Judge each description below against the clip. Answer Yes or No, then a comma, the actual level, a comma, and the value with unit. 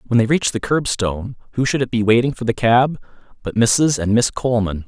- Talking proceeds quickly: Yes, fast, 210 wpm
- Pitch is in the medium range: No, low, 120 Hz